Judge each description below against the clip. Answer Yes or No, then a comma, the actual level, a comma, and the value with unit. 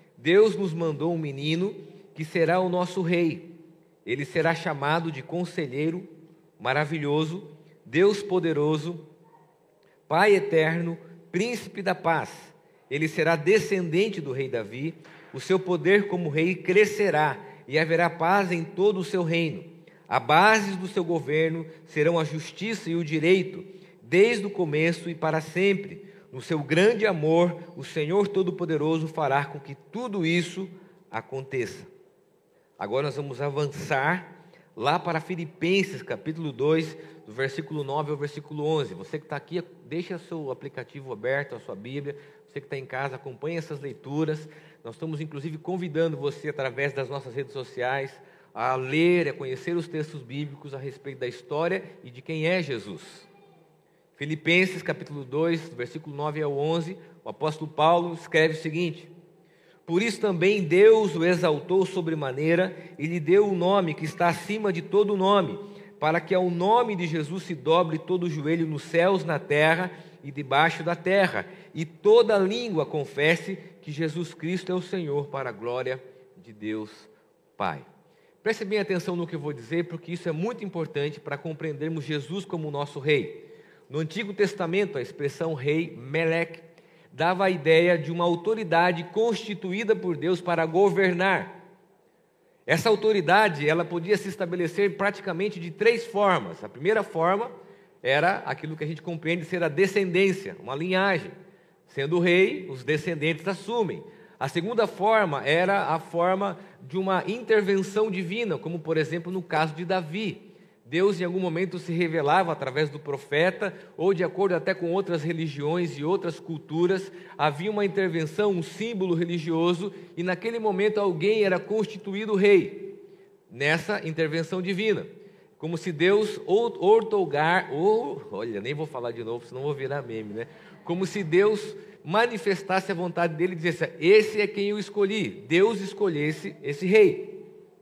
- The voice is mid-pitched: Yes, medium, 175 Hz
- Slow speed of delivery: No, average, 155 wpm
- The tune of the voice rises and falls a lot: No, average, 3.8 semitones